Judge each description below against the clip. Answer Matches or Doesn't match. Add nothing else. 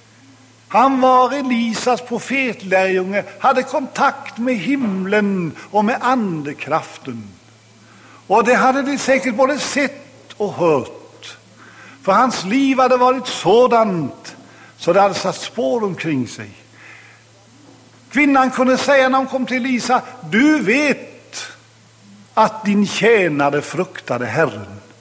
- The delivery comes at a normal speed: Doesn't match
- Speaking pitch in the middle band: Doesn't match